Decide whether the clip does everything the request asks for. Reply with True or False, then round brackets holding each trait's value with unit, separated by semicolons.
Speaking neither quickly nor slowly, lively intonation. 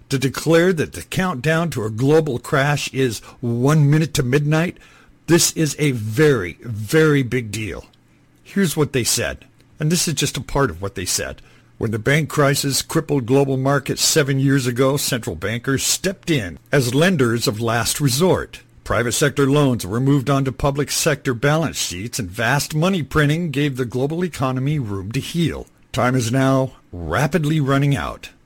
False (170 wpm; 3.6 semitones)